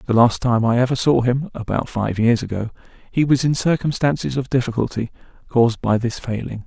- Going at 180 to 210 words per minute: Yes, average, 190 wpm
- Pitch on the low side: Yes, low, 125 Hz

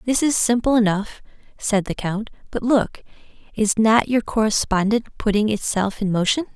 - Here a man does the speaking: No, female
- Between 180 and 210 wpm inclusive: No, average, 155 wpm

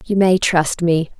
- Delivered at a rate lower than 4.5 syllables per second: Yes, 3.9 syllables/s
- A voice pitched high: No, medium, 175 Hz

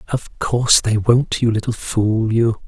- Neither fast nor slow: Yes, average, 180 wpm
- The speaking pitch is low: Yes, low, 115 Hz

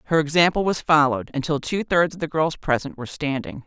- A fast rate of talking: Yes, fast, 215 wpm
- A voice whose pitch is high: No, medium, 155 Hz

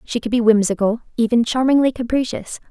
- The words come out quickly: No, slow, 135 wpm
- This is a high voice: Yes, high, 235 Hz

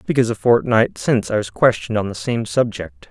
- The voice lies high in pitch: No, low, 110 Hz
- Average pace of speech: No, fast, 210 wpm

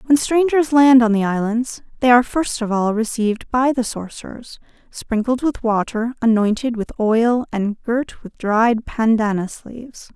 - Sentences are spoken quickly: No, average, 160 wpm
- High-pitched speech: Yes, high, 235 Hz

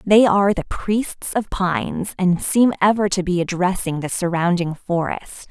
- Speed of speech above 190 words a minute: No, average, 165 wpm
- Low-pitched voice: No, medium, 185 Hz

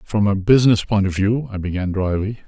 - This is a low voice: Yes, low, 100 Hz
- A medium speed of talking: No, fast, 220 wpm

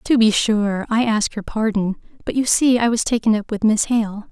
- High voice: Yes, high, 220 Hz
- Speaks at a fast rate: Yes, fast, 235 wpm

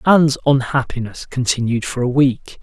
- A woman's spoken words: No, male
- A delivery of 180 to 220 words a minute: No, slow, 135 wpm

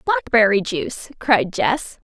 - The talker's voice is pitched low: No, high, 240 Hz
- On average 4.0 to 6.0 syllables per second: No, 3.7 syllables/s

